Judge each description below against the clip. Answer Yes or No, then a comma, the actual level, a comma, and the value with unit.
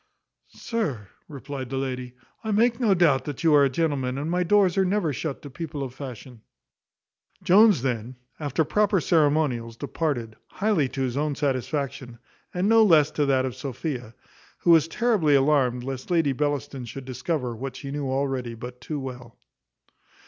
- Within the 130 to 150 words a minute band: No, average, 170 wpm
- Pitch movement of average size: Yes, average, 4.3 semitones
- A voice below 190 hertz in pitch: Yes, medium, 140 Hz